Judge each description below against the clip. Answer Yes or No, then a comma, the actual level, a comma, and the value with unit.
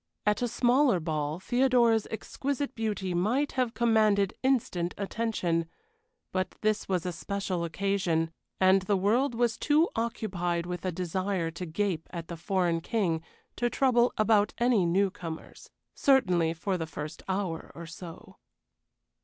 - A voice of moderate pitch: No, high, 195 Hz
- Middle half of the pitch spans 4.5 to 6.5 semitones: Yes, average, 5.0 semitones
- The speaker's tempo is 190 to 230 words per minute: No, average, 145 wpm